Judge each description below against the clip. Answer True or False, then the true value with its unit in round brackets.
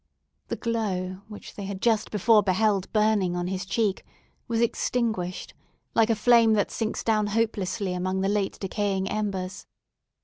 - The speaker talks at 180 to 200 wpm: False (150 wpm)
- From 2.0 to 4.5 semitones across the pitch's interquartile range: True (2.7 semitones)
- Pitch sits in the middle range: False (205 Hz)